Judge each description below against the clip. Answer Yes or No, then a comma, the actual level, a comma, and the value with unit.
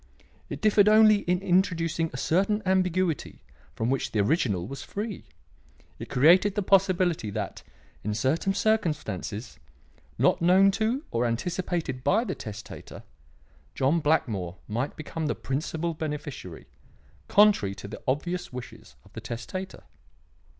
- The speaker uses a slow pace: Yes, slow, 130 wpm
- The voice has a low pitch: No, medium, 165 Hz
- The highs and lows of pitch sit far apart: Yes, wide, 7.2 semitones